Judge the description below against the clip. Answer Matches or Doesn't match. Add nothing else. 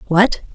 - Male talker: Doesn't match